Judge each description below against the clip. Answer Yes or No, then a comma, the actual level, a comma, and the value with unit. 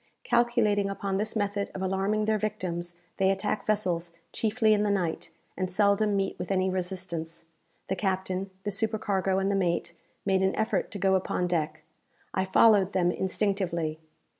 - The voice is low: No, high, 195 Hz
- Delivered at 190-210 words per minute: No, average, 165 wpm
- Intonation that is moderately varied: No, narrow, 2.1 semitones